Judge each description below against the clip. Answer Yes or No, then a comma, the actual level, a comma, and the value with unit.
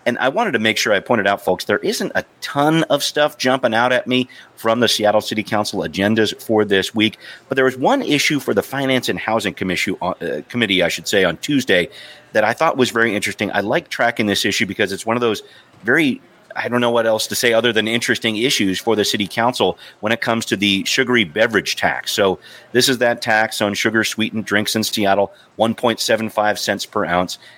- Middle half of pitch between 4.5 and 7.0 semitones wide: No, average, 2.8 semitones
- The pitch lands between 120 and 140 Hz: No, low, 110 Hz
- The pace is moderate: No, fast, 220 wpm